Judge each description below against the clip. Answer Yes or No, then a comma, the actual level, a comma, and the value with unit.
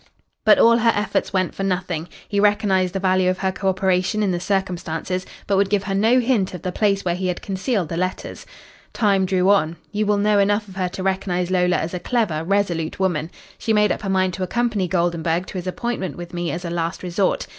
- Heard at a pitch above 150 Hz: Yes, high, 190 Hz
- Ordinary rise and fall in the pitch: No, narrow, 2.2 semitones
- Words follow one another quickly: Yes, fast, 230 wpm